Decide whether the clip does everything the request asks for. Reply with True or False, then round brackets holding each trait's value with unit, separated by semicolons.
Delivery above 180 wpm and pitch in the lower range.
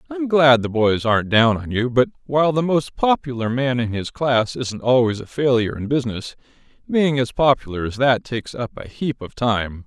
True (205 wpm; 125 Hz)